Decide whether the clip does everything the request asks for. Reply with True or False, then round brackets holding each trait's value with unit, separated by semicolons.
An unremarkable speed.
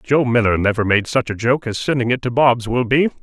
False (260 wpm)